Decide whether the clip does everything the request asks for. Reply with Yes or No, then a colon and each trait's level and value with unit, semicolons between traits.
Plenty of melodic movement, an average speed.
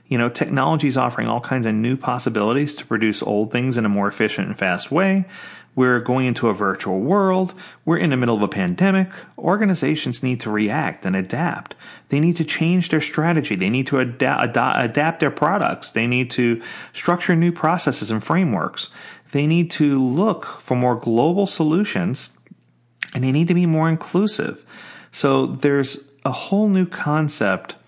Yes: wide, 6.3 semitones; average, 175 wpm